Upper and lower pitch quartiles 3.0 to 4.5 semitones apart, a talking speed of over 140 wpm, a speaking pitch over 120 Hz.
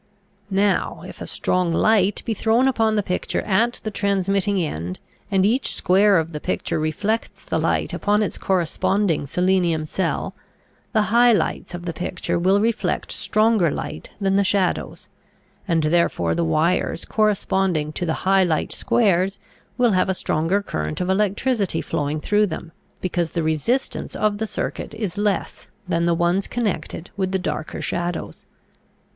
Yes: average, 3.6 semitones; average, 160 wpm; high, 190 Hz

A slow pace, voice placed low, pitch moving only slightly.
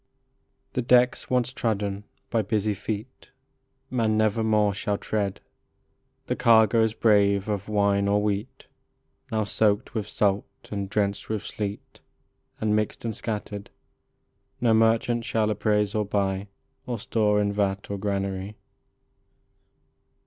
Yes: slow, 125 wpm; low, 105 Hz; narrow, 1.7 semitones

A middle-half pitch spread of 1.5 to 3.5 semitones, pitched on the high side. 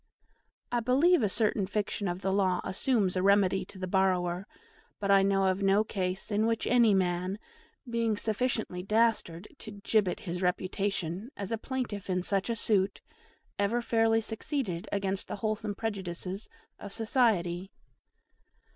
Yes: average, 3.0 semitones; high, 200 Hz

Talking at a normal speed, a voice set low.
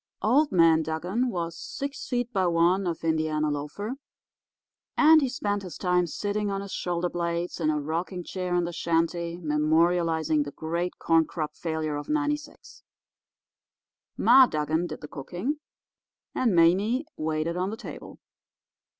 No: average, 150 wpm; medium, 175 Hz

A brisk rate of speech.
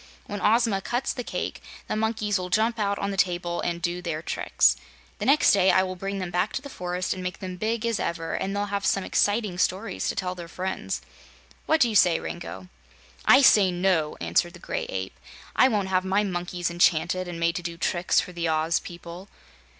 Yes: fast, 220 wpm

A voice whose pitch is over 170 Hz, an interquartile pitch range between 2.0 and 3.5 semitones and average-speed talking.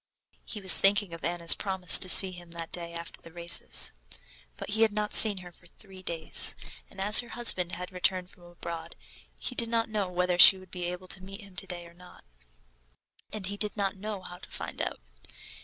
No: medium, 185 Hz; narrow, 2.6 semitones; fast, 215 wpm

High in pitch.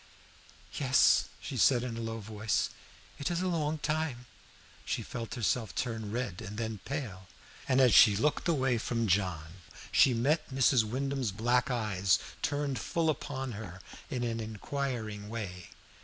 No: low, 120 Hz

